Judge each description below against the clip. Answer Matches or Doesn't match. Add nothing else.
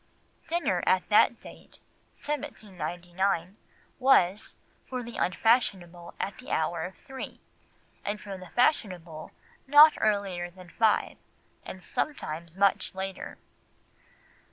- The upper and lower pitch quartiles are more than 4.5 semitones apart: Matches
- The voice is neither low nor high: Doesn't match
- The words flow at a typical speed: Doesn't match